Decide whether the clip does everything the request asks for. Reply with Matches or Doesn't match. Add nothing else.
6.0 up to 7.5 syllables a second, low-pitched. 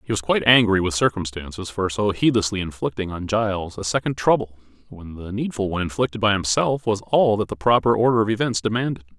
Matches